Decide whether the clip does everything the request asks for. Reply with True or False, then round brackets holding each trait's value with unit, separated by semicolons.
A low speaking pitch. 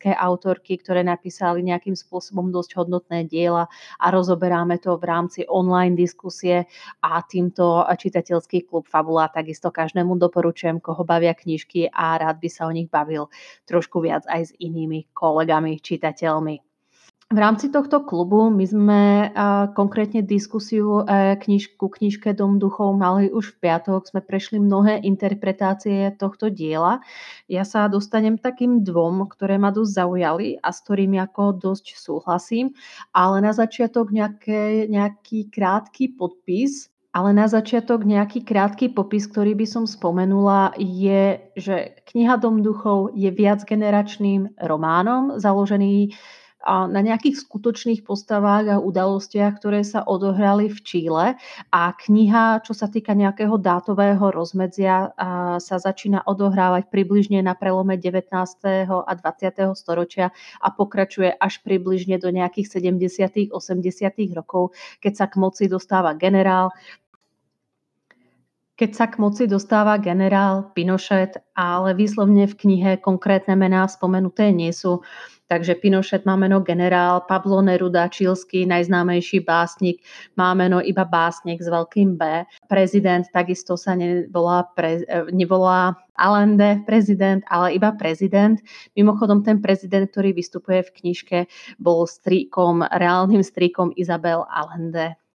False (190 Hz)